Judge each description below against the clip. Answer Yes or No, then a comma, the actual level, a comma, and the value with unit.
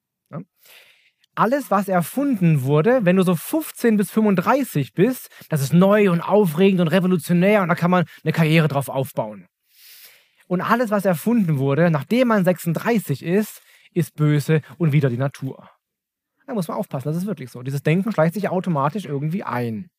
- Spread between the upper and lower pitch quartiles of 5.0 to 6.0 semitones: Yes, average, 5.3 semitones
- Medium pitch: Yes, medium, 180 Hz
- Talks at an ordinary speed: Yes, average, 170 wpm